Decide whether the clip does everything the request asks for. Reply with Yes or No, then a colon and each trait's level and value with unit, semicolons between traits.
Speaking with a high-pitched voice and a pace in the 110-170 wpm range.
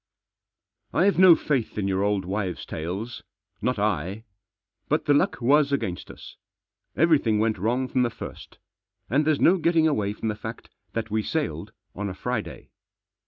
No: low, 115 Hz; average, 165 wpm